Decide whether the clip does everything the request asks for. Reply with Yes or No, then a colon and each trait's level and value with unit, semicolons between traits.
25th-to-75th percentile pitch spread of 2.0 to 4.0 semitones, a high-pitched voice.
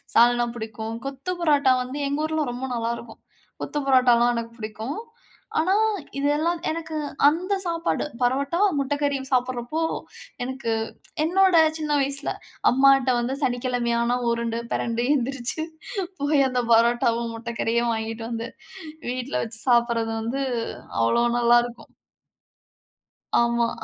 Yes: average, 3.2 semitones; high, 245 Hz